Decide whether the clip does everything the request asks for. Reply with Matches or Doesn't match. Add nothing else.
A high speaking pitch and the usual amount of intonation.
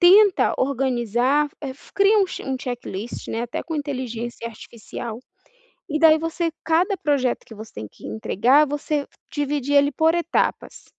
Matches